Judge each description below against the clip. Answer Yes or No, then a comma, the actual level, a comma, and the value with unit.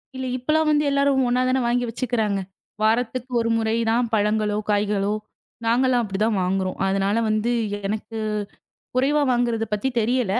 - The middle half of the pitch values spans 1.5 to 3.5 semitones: Yes, average, 3.2 semitones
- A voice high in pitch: Yes, high, 230 Hz